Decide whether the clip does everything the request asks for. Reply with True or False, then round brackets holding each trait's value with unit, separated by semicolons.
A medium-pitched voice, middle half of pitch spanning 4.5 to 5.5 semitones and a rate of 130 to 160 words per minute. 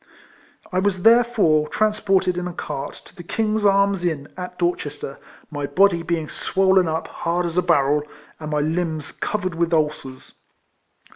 False (175 Hz; 3.9 semitones; 155 wpm)